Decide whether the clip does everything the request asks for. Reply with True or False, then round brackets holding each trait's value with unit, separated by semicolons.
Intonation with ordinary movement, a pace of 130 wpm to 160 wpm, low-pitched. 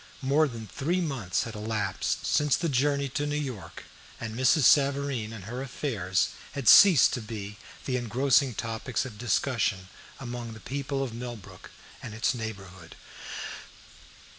True (4.1 semitones; 145 wpm; 120 Hz)